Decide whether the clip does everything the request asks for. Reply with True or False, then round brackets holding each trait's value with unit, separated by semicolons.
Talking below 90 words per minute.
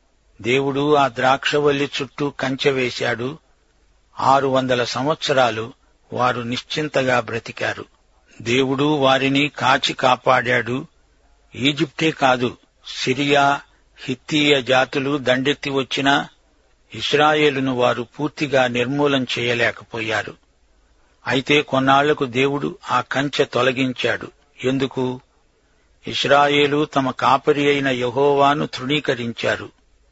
True (80 wpm)